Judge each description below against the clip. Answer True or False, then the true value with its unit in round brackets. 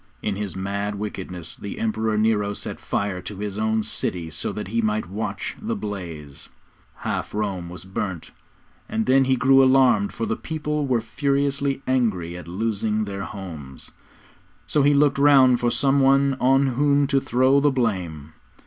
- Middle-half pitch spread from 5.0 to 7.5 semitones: True (5.5 semitones)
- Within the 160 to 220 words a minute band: True (165 wpm)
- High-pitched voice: False (110 Hz)